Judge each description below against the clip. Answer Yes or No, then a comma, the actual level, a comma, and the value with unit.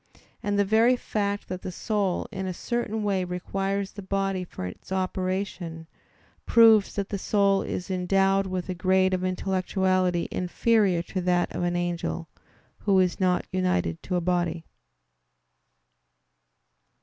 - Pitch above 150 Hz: Yes, medium, 185 Hz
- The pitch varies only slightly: Yes, narrow, 1.8 semitones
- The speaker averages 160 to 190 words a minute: No, average, 145 wpm